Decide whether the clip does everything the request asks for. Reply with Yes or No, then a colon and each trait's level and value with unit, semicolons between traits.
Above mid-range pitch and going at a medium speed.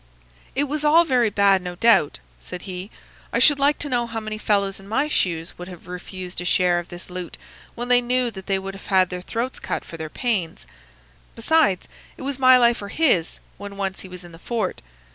No: high, 200 Hz; fast, 220 wpm